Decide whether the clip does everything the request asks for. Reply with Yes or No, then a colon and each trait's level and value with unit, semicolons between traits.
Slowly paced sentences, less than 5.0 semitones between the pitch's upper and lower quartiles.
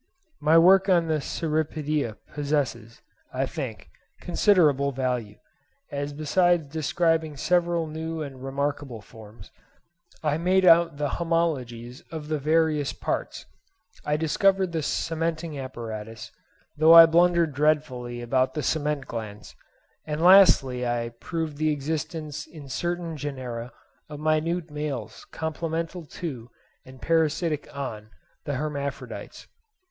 Yes: slow, 115 wpm; average, 3.8 semitones